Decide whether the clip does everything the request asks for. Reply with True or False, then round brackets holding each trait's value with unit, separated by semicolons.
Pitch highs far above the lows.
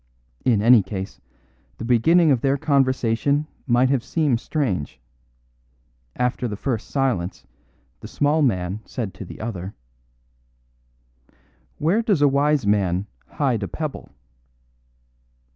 True (5.7 semitones)